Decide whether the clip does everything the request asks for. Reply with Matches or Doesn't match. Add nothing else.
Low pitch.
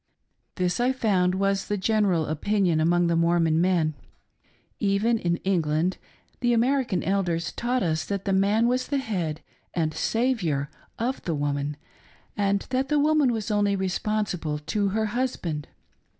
Doesn't match